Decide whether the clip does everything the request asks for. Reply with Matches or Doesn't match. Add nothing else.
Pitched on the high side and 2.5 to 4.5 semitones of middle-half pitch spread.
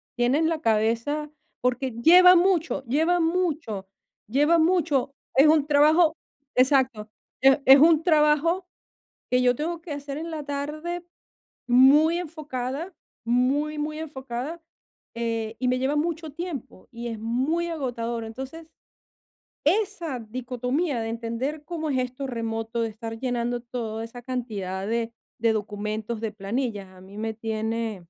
Doesn't match